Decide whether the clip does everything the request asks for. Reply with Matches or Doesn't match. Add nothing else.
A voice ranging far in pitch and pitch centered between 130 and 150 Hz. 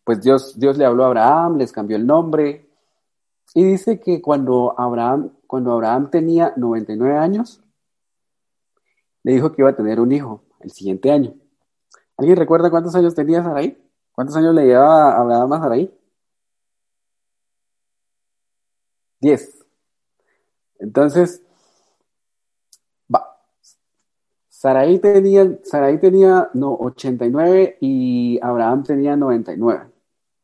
Matches